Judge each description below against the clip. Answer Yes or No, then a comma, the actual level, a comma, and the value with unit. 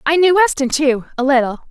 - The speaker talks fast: Yes, fast, 210 wpm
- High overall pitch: Yes, very high, 290 Hz